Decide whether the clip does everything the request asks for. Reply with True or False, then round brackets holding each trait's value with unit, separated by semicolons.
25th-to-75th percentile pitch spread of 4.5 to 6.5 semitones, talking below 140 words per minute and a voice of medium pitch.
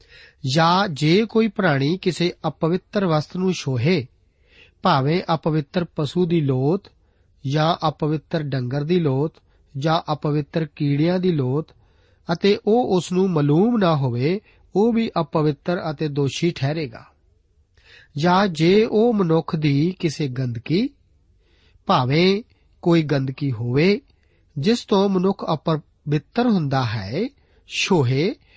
True (4.9 semitones; 115 wpm; 160 Hz)